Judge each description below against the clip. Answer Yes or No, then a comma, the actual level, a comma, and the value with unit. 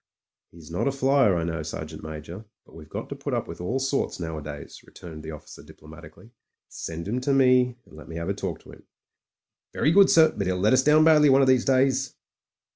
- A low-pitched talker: Yes, low, 105 Hz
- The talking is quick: Yes, fast, 220 wpm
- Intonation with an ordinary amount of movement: No, wide, 8.6 semitones